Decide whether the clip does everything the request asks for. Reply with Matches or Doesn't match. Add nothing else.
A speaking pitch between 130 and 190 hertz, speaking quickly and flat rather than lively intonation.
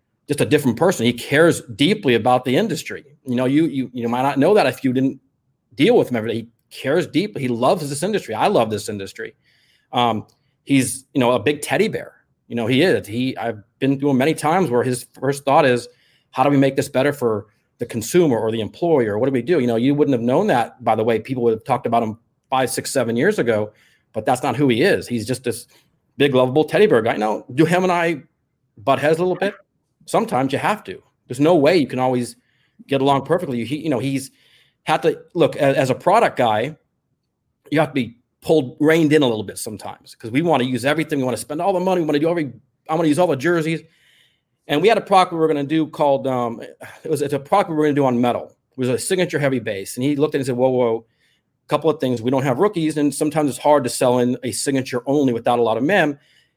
Doesn't match